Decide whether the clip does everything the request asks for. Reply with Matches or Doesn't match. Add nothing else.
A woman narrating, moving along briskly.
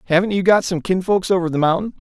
Doesn't match